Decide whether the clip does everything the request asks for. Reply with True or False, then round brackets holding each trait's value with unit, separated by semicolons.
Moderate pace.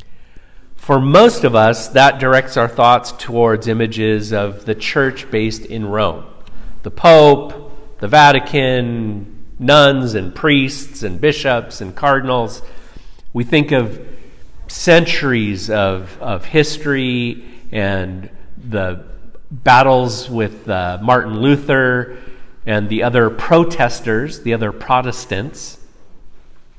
False (110 wpm)